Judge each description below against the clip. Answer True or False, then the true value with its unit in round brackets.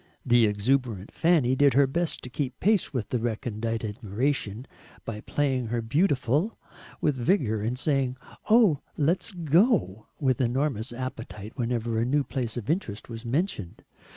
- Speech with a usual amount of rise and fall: True (4.3 semitones)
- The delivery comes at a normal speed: True (150 wpm)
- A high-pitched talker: False (125 Hz)